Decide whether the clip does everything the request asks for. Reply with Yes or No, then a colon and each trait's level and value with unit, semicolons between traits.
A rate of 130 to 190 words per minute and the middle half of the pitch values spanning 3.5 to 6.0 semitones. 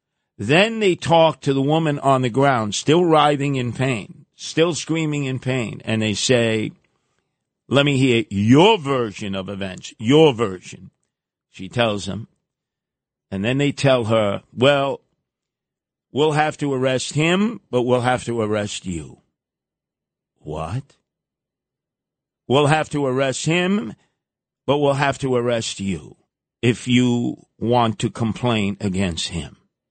Yes: slow, 135 wpm; average, 4.7 semitones